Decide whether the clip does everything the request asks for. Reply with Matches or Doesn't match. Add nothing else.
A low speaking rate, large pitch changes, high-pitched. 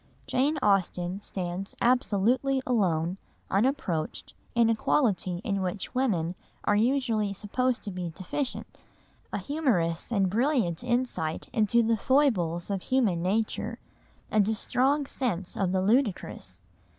Matches